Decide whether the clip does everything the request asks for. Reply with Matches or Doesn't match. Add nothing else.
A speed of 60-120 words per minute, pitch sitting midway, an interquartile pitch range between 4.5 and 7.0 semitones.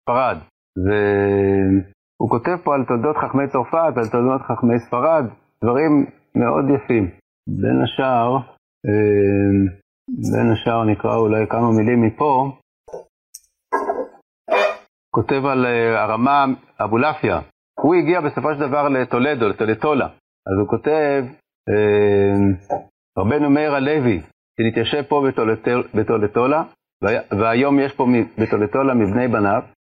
Doesn't match